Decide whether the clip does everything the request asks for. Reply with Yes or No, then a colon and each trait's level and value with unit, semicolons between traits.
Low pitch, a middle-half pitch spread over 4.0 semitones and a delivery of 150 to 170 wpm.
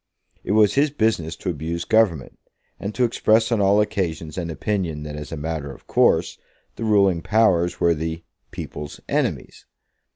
Yes: very low, 85 Hz; average, 4.9 semitones; average, 165 wpm